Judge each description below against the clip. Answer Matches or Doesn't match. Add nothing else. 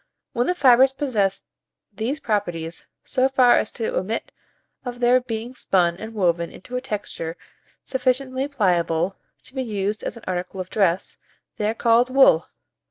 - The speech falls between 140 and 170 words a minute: Matches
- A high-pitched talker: Matches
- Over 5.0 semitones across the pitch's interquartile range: Matches